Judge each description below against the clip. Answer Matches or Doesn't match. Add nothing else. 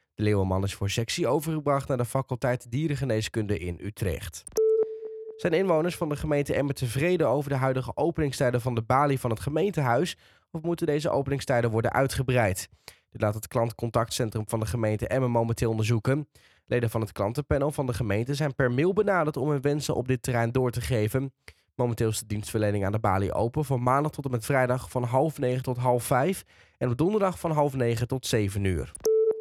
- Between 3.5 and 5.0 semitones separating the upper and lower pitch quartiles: Matches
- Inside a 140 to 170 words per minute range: Doesn't match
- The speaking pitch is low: Matches